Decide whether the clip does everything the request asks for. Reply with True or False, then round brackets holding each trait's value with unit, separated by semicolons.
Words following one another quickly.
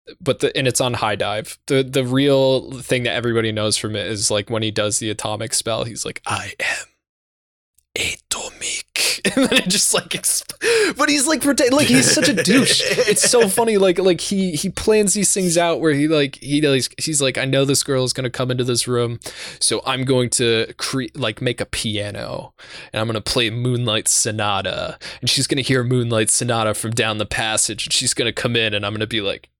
True (215 wpm)